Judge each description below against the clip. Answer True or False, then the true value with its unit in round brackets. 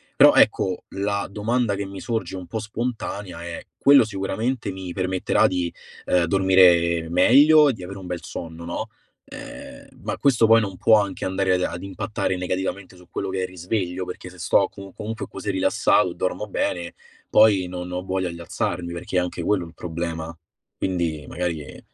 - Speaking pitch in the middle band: False (95 Hz)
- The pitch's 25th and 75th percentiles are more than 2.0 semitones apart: True (2.5 semitones)